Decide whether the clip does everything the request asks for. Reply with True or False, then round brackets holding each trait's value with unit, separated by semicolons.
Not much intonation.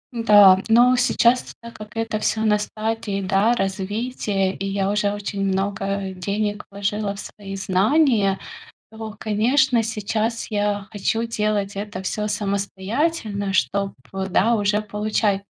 True (2.1 semitones)